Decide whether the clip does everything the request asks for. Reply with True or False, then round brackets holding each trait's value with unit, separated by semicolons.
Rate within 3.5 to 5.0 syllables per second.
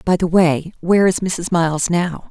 True (4.8 syllables/s)